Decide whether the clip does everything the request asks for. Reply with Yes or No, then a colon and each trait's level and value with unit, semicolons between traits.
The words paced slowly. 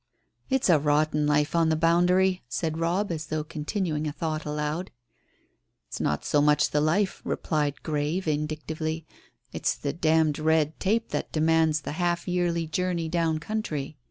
No: average, 160 wpm